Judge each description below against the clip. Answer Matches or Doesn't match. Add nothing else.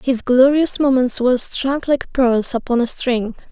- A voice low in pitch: Doesn't match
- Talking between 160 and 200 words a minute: Matches